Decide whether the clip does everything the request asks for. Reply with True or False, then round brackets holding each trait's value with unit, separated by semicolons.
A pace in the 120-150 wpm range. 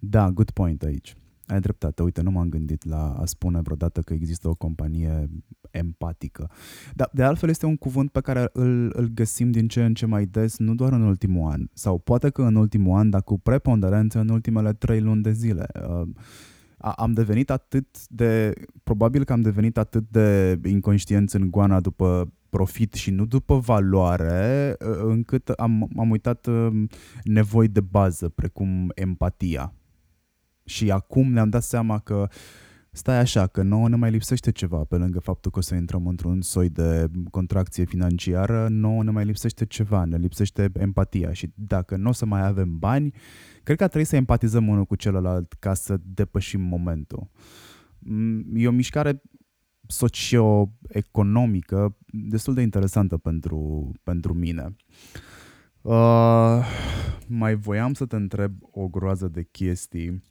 False (160 wpm)